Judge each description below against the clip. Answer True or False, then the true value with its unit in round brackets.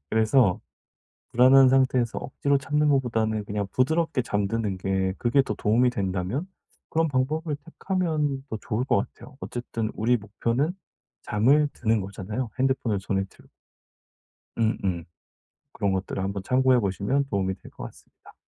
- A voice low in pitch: True (120 Hz)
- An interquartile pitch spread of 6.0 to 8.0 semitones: False (5.1 semitones)